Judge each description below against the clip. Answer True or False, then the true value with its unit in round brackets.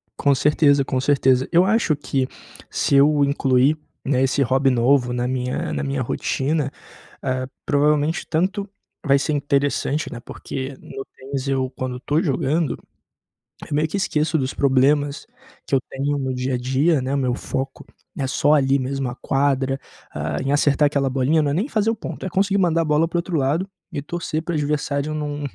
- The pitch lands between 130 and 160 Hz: True (140 Hz)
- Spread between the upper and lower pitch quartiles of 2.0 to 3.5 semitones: True (2.5 semitones)